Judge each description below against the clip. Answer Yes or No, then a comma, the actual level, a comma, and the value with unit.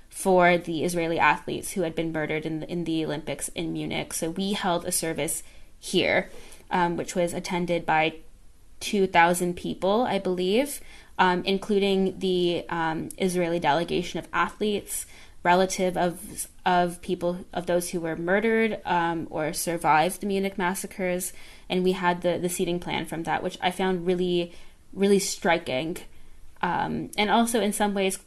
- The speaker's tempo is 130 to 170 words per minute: Yes, average, 160 wpm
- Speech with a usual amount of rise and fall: No, narrow, 2.1 semitones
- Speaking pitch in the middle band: Yes, medium, 175 Hz